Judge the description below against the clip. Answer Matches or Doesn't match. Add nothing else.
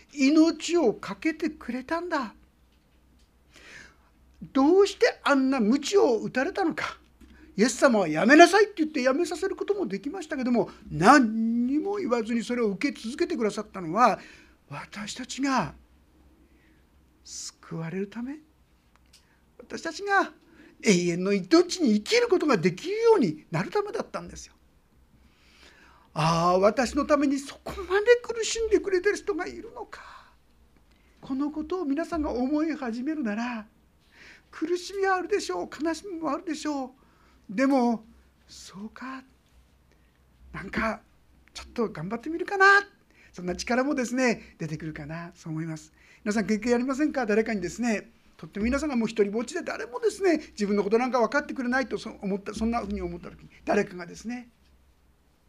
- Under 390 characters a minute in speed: Matches